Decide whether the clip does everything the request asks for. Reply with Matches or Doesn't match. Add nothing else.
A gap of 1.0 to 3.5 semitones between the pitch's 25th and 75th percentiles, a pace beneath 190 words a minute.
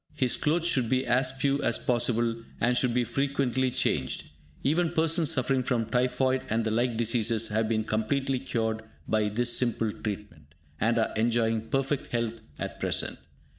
Matches